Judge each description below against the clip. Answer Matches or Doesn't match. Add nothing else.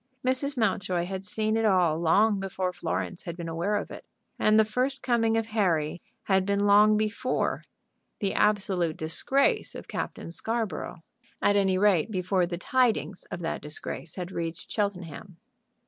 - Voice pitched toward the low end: Doesn't match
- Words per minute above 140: Matches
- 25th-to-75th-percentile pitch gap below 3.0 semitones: Doesn't match